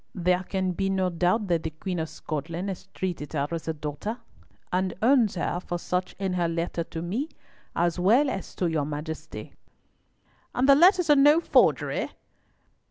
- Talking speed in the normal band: Yes, average, 175 wpm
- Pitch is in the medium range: Yes, medium, 180 Hz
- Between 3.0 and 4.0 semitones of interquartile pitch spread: Yes, average, 3.4 semitones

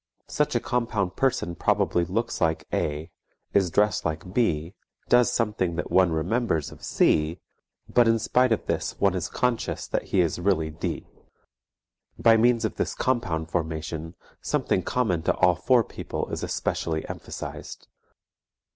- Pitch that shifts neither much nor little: No, wide, 6.2 semitones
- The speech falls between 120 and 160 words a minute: Yes, average, 150 wpm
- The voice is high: No, very low, 95 Hz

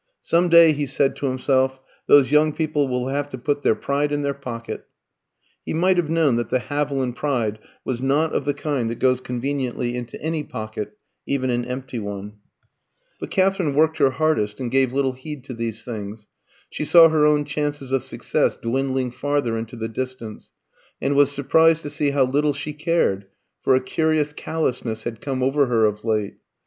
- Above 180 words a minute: Yes, average, 190 wpm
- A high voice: No, low, 135 Hz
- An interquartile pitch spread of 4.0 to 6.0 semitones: No, average, 3.4 semitones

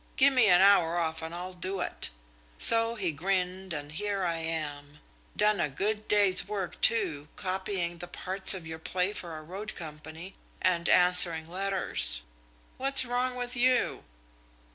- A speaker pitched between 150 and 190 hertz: Yes, medium, 185 Hz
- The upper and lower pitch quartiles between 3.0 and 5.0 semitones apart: Yes, average, 4.0 semitones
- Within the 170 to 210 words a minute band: No, average, 160 wpm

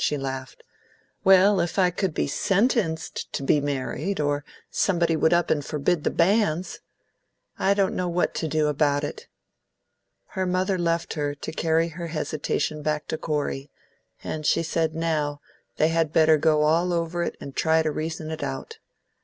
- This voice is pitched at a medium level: Yes, medium, 160 Hz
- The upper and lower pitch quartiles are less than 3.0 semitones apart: Yes, narrow, 2.6 semitones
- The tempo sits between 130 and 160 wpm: No, average, 170 wpm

